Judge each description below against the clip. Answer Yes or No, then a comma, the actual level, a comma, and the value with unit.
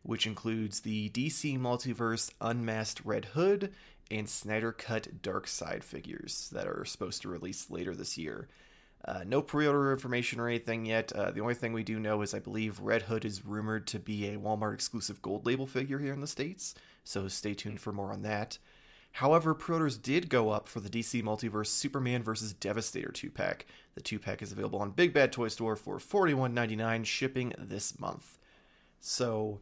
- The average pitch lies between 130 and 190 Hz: No, low, 115 Hz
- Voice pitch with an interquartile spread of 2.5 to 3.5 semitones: Yes, average, 3.1 semitones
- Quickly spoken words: No, average, 195 wpm